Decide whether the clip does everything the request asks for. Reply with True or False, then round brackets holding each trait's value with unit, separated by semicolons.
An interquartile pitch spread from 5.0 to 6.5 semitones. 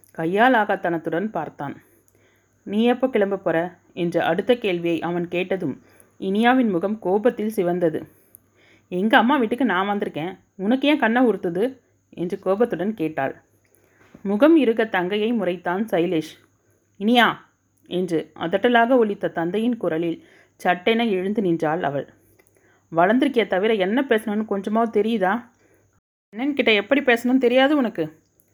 True (5.5 semitones)